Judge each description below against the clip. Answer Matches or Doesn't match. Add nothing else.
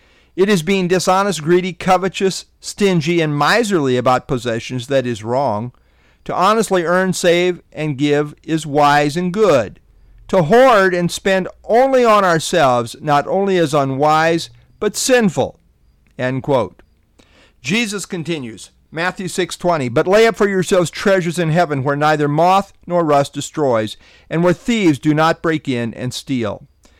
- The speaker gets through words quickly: Doesn't match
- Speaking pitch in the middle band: Matches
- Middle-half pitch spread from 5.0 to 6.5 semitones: Matches